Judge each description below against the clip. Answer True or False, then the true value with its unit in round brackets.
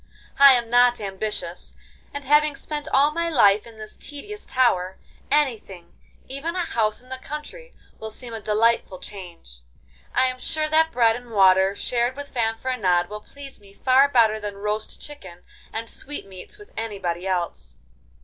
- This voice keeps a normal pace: True (155 wpm)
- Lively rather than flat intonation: True (5.8 semitones)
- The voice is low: False (230 Hz)